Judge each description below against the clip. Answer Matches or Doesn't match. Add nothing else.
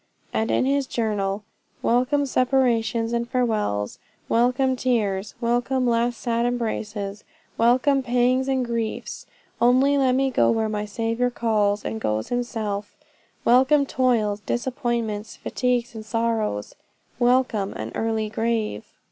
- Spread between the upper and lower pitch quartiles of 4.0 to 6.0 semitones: Doesn't match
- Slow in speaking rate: Matches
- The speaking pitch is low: Doesn't match